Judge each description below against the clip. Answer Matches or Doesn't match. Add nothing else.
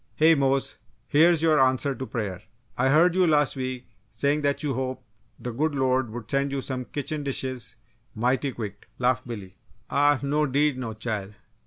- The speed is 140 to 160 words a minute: Doesn't match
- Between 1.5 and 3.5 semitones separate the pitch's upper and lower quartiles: Matches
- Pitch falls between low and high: Doesn't match